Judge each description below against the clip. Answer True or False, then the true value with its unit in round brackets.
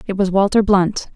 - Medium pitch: False (195 Hz)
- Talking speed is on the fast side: True (210 wpm)